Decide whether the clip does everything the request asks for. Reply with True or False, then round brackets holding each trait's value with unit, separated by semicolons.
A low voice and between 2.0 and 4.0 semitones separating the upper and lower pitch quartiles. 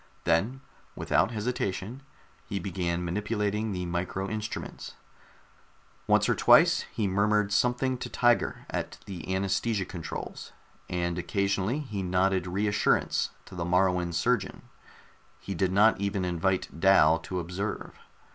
True (95 Hz; 2.8 semitones)